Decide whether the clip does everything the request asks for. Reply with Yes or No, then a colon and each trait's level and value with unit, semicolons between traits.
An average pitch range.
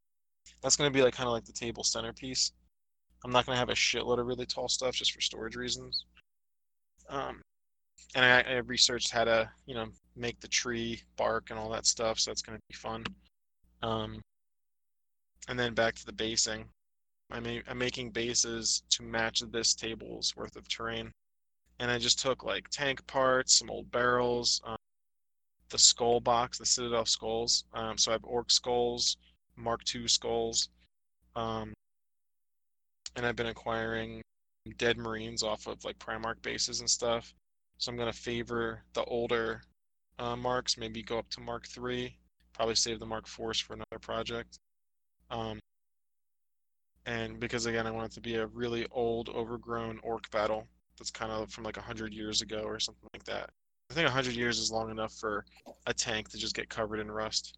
No: narrow, 1.5 semitones